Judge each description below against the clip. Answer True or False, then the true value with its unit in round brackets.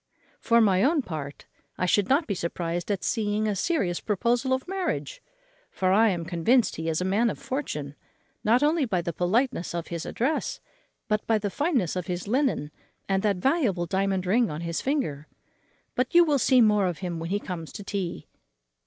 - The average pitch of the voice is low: False (200 Hz)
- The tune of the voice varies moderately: False (6.2 semitones)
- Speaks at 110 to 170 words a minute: False (195 wpm)